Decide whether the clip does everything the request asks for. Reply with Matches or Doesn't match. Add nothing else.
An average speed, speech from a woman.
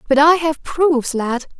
Matches